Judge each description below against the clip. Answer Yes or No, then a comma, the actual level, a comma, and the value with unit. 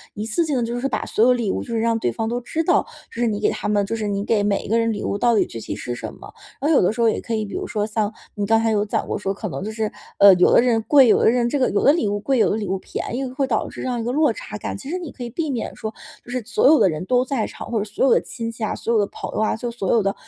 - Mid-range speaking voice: No, high, 225 Hz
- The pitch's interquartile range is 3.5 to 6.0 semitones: No, average, 3.0 semitones